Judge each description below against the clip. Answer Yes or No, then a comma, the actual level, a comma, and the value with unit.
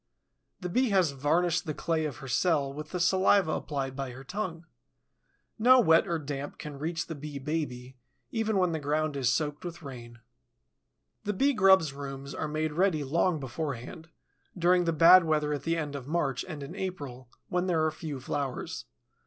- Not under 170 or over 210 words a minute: Yes, average, 185 wpm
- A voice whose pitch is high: No, medium, 155 Hz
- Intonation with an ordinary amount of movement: Yes, average, 4.0 semitones